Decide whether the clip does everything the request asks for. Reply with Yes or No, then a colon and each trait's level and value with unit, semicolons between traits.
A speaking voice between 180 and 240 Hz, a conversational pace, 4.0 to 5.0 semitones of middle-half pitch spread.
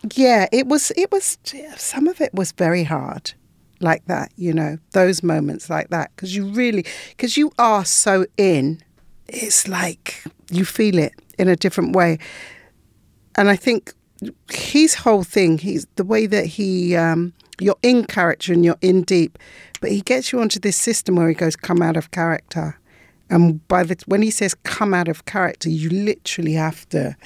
Yes: medium, 185 Hz; average, 185 wpm; average, 4.5 semitones